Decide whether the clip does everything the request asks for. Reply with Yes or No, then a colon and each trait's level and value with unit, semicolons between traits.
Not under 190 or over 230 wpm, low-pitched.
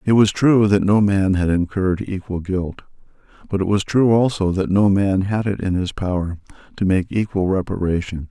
Yes: average, 195 wpm; very low, 95 Hz